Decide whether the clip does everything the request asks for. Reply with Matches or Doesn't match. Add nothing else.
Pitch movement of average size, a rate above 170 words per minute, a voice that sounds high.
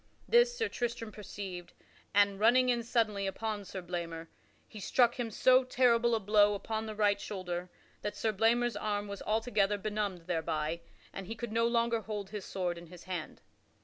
Matches